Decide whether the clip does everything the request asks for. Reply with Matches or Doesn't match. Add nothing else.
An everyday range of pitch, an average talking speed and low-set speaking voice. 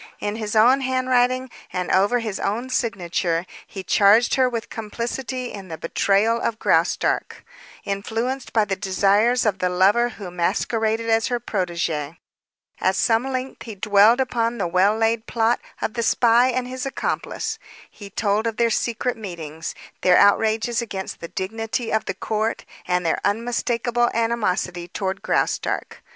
Doesn't match